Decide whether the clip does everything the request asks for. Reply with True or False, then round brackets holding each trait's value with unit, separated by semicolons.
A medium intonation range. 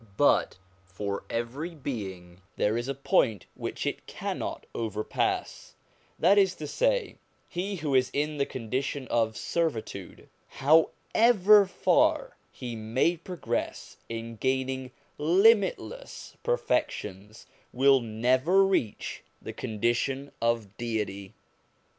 False (7.1 semitones)